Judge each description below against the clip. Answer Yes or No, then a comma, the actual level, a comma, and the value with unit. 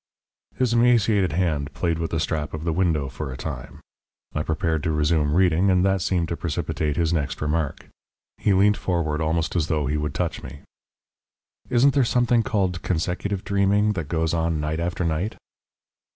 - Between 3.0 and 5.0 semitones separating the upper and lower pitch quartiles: Yes, average, 3.9 semitones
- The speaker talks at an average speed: Yes, average, 180 wpm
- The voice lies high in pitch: No, very low, 85 Hz